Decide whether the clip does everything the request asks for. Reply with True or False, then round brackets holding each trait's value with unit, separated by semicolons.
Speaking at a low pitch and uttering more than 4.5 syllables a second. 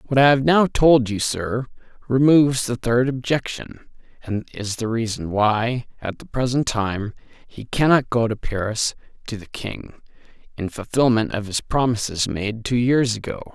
False (120 Hz; 4.4 syllables/s)